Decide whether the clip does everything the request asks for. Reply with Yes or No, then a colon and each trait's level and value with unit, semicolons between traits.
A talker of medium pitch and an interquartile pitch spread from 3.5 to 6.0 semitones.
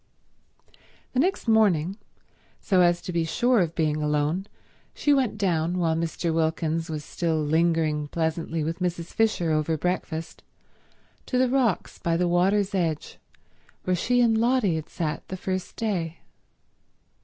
Yes: medium, 170 Hz; average, 3.8 semitones